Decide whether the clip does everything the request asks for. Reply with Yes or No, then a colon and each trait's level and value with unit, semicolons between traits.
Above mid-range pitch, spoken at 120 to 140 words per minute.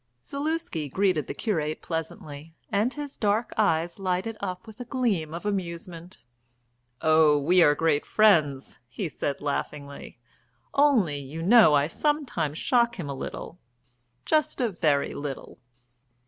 No: medium, 175 Hz; slow, 135 wpm